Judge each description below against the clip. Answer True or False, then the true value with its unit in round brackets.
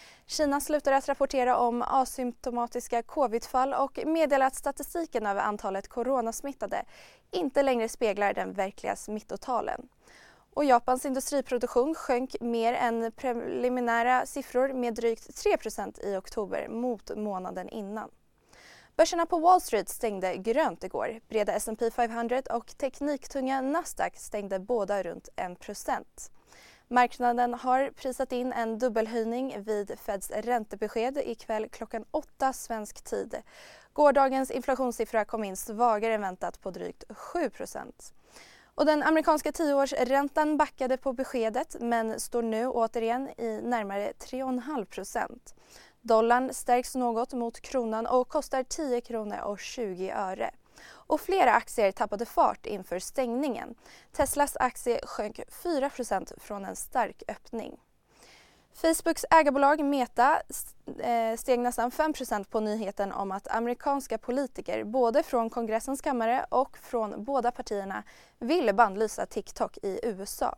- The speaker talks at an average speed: False (120 wpm)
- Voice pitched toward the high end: True (245 Hz)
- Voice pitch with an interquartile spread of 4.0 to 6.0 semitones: False (3.4 semitones)